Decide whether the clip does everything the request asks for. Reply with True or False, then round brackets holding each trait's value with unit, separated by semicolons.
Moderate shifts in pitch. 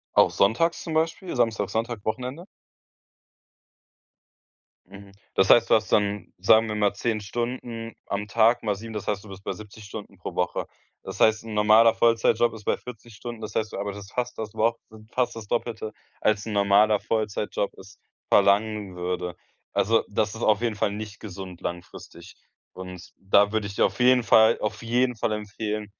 False (2.2 semitones)